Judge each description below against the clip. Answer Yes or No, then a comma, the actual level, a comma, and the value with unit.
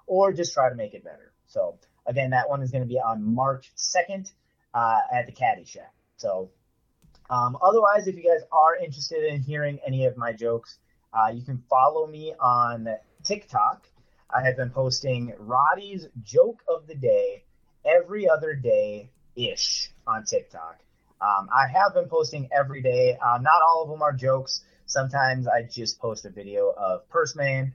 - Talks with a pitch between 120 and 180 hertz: Yes, medium, 140 Hz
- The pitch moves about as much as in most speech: No, wide, 6.6 semitones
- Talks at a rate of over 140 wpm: Yes, average, 175 wpm